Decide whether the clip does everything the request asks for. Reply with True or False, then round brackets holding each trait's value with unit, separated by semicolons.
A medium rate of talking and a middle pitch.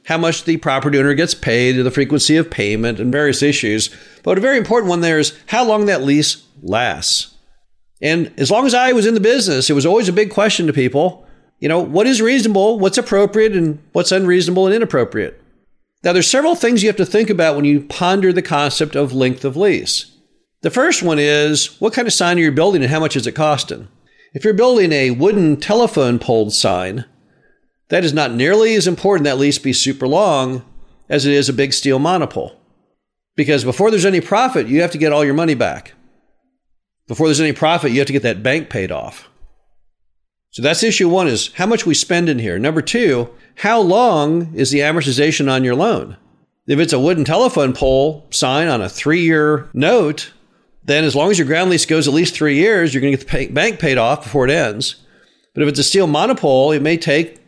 False (215 wpm; 155 Hz)